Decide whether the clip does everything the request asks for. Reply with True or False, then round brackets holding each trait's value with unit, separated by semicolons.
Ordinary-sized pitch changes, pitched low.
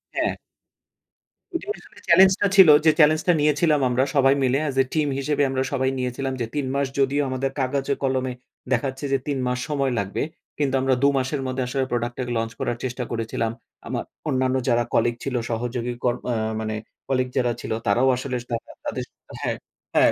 False (2.2 semitones; 130 Hz)